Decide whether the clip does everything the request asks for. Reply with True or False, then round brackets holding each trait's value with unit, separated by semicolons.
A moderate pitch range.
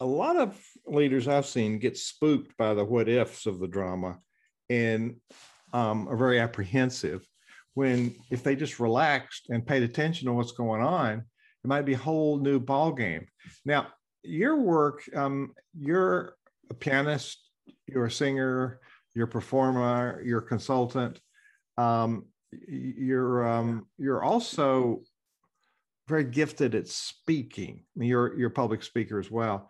True (3.6 semitones)